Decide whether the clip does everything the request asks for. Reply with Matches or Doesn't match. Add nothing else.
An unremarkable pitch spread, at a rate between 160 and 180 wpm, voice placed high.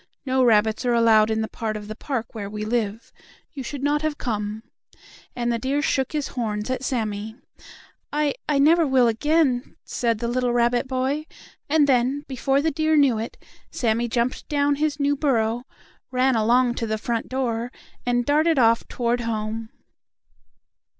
Matches